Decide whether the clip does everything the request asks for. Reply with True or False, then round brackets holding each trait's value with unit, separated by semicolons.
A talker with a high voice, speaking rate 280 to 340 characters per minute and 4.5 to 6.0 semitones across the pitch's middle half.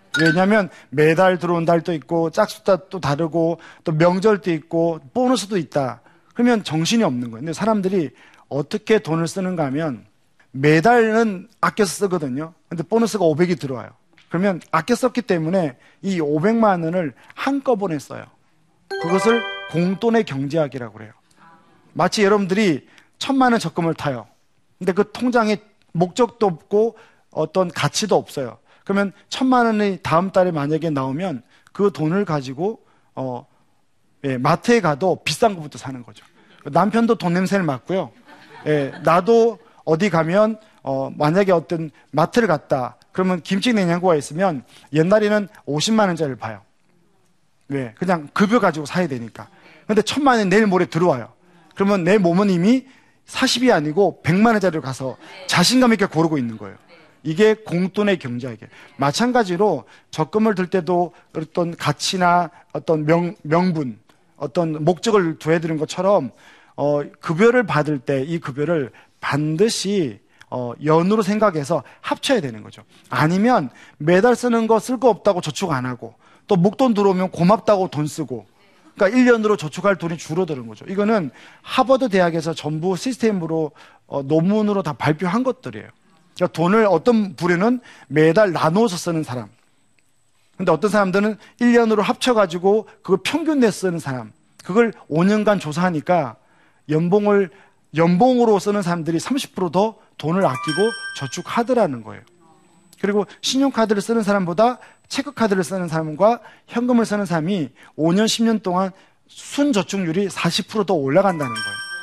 False (180 Hz; 315 characters per minute; 5.5 semitones)